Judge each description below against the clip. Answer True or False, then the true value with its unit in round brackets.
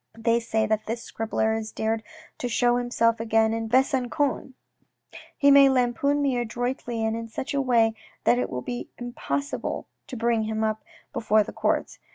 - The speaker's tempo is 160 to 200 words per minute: True (175 wpm)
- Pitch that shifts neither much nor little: False (2.1 semitones)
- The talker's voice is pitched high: True (230 Hz)